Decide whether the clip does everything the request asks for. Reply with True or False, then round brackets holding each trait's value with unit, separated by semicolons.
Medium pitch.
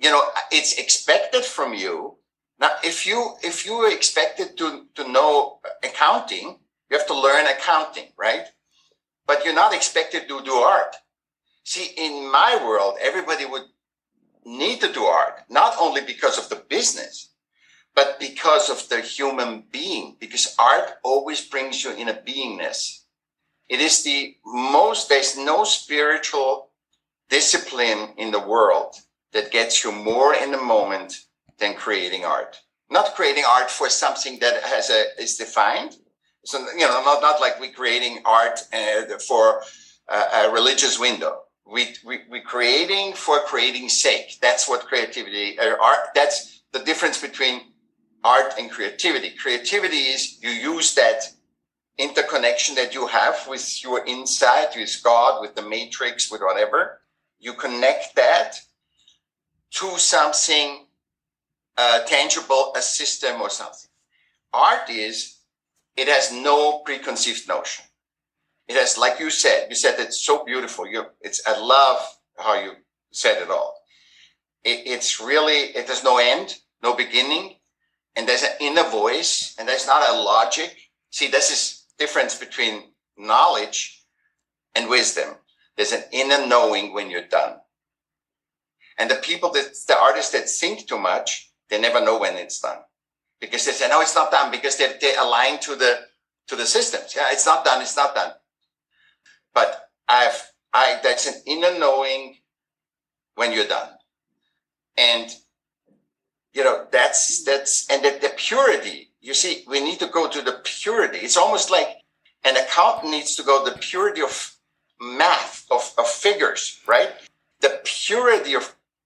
True (160 Hz)